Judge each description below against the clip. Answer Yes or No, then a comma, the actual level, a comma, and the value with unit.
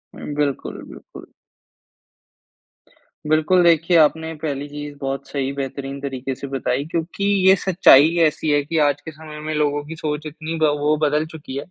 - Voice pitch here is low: No, medium, 150 Hz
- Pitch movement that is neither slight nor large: No, narrow, 2.2 semitones